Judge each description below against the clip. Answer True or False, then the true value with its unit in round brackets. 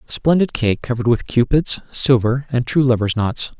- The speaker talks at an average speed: True (165 wpm)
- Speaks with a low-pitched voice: True (125 Hz)